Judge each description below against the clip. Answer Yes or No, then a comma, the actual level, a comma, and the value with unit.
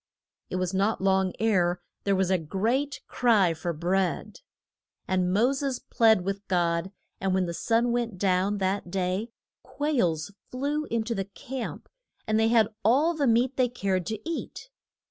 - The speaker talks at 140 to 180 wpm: Yes, average, 165 wpm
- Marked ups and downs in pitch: No, average, 4.4 semitones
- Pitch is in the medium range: No, high, 200 Hz